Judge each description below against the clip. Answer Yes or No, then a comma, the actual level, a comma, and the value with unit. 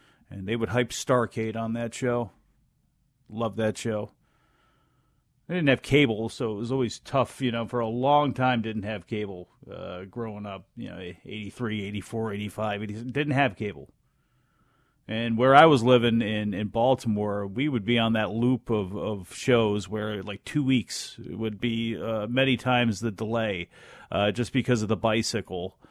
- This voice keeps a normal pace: Yes, average, 170 wpm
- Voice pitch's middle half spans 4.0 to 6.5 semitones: No, average, 2.7 semitones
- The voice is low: Yes, low, 115 Hz